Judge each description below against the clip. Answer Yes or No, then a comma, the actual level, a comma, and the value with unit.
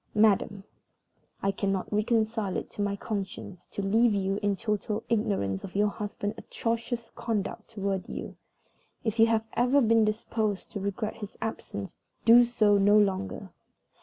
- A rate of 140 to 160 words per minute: Yes, average, 150 wpm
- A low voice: No, high, 210 Hz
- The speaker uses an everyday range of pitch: No, narrow, 2.2 semitones